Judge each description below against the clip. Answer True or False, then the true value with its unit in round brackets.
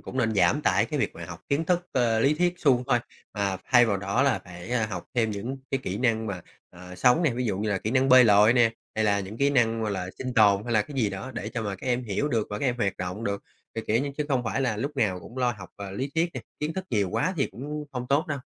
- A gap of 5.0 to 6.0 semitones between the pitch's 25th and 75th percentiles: False (4.6 semitones)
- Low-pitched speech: True (115 Hz)